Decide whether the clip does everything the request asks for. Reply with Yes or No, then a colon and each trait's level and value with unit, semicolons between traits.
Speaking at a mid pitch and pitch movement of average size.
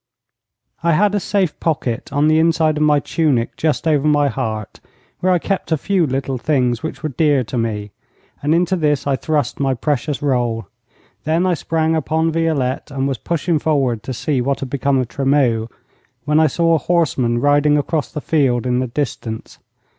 Yes: medium, 145 Hz; average, 3.8 semitones